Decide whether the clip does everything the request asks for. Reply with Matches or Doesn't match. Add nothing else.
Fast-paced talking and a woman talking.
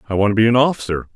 Doesn't match